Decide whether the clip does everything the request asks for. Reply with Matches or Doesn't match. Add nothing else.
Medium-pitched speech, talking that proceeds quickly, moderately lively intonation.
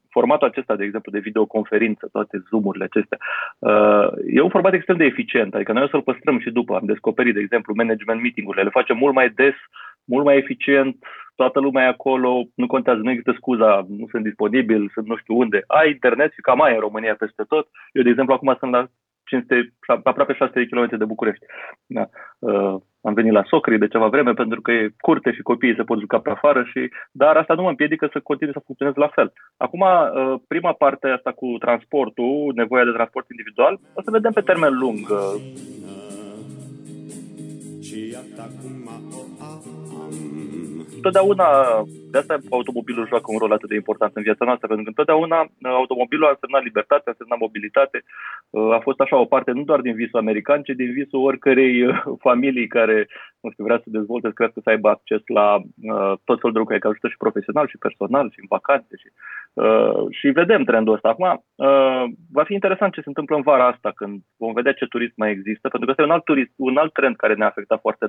Doesn't match